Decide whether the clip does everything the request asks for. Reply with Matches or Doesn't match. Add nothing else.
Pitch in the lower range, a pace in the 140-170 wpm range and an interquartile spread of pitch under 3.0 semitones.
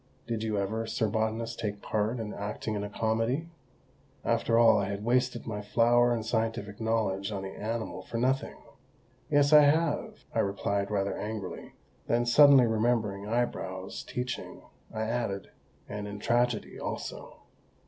Matches